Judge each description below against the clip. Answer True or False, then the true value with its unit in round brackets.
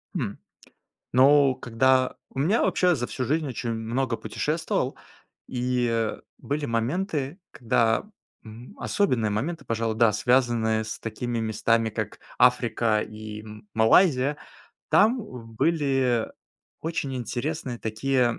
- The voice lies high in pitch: False (125 Hz)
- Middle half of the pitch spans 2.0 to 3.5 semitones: False (3.9 semitones)